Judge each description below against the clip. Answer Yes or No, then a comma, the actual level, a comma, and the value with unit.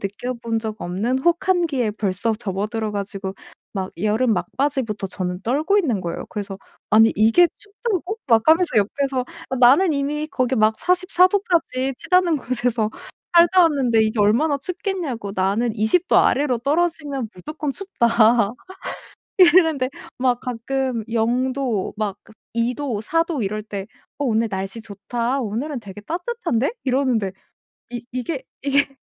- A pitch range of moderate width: No, wide, 5.7 semitones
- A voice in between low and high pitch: No, high, 245 Hz